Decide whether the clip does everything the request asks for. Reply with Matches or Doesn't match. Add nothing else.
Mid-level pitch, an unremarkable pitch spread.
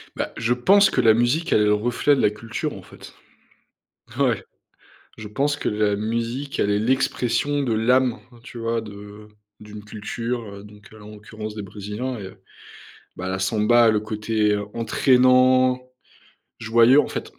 Doesn't match